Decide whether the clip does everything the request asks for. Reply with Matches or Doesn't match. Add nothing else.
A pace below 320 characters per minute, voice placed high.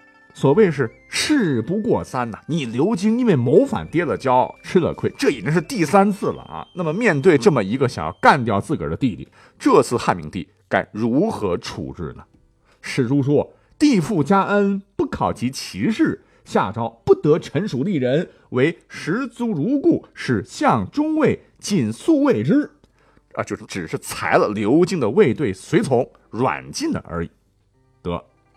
Matches